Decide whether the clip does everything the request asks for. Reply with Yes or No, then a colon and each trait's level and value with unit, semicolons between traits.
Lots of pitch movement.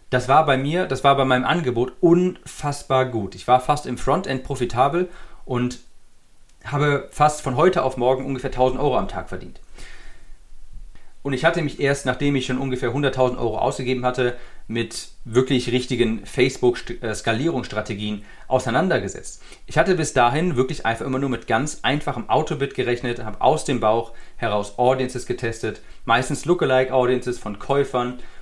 No: narrow, 2.5 semitones